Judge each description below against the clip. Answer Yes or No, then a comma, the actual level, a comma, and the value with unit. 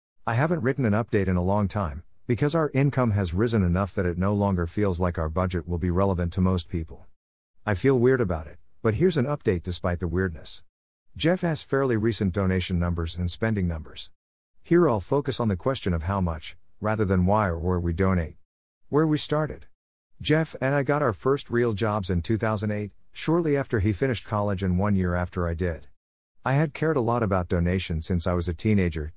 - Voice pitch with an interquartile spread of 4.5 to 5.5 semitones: Yes, average, 5.2 semitones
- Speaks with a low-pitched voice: Yes, very low, 95 Hz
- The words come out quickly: Yes, fast, 210 wpm